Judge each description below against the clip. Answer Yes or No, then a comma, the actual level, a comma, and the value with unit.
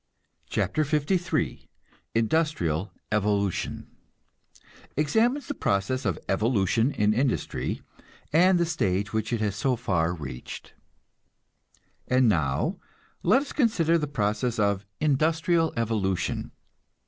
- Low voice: Yes, low, 115 Hz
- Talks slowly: Yes, slow, 105 wpm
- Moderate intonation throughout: No, wide, 7.7 semitones